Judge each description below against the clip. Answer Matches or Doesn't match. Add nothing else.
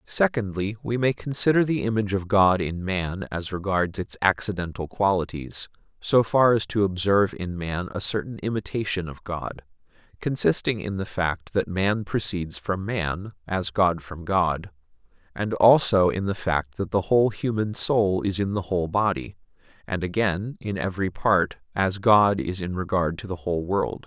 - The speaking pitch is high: Doesn't match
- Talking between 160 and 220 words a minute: Matches